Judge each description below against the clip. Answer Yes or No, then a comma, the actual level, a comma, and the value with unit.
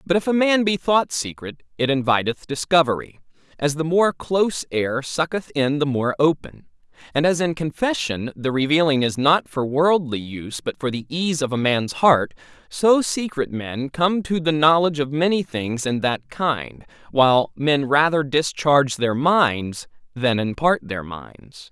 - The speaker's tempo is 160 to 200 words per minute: Yes, average, 170 wpm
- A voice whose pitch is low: No, medium, 145 Hz